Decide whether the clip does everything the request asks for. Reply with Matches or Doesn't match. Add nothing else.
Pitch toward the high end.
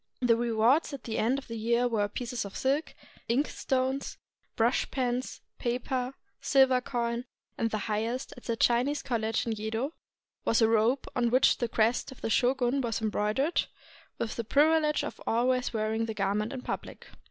Matches